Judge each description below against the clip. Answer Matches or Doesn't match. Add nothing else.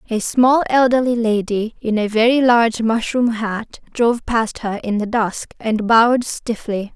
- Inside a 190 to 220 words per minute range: Doesn't match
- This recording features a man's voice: Doesn't match